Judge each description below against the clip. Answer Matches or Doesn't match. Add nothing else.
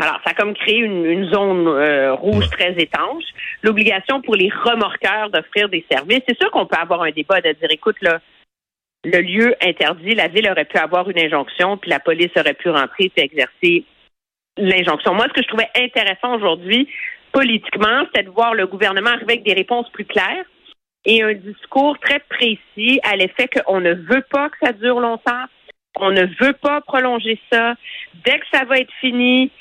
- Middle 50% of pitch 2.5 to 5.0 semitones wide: Doesn't match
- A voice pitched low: Doesn't match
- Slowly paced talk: Doesn't match